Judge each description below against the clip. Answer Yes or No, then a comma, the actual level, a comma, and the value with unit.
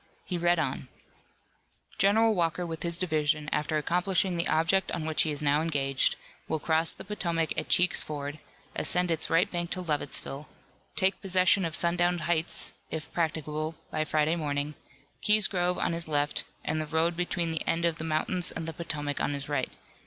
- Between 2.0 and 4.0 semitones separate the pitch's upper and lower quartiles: Yes, narrow, 2.4 semitones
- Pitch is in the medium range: Yes, medium, 165 Hz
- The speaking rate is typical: Yes, average, 180 wpm